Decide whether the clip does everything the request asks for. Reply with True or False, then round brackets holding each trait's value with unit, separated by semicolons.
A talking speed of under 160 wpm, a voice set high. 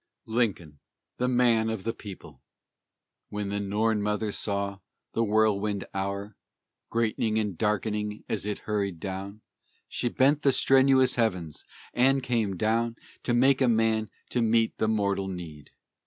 False (140 wpm; 110 Hz)